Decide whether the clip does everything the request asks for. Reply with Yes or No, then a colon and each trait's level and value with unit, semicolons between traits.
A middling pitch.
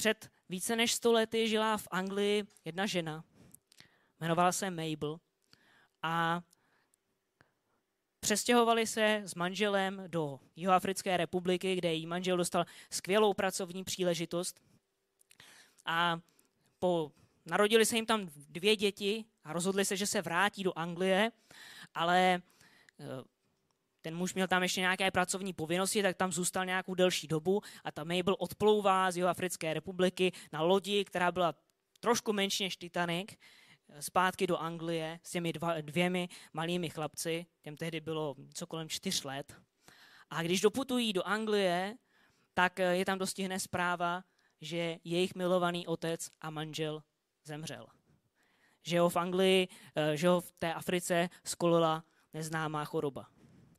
Yes: medium, 180 Hz